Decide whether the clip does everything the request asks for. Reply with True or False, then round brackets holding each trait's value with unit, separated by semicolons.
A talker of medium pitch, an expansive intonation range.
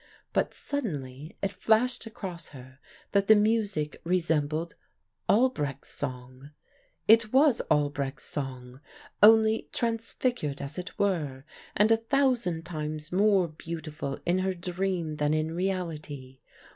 True (170 Hz; 6.4 semitones)